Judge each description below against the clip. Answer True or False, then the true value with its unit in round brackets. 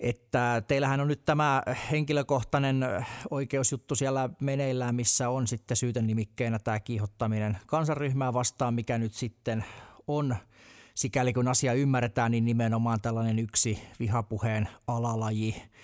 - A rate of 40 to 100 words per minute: False (120 wpm)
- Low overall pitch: True (120 Hz)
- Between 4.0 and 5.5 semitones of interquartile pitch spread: False (2.9 semitones)